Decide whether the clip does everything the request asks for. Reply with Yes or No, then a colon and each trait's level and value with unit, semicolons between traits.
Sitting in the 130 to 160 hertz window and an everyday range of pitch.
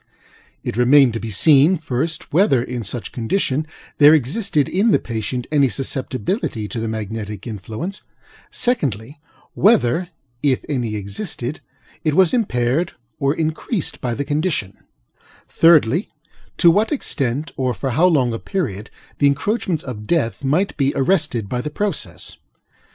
No: medium, 140 Hz; wide, 5.9 semitones